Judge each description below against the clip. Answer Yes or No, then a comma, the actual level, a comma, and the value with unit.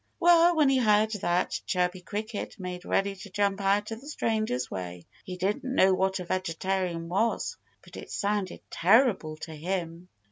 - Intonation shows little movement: No, average, 3.4 semitones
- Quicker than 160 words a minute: Yes, average, 170 wpm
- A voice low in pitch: No, high, 195 Hz